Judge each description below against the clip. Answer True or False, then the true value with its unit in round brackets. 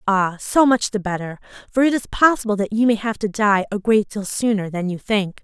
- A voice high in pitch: True (210 Hz)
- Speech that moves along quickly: True (245 wpm)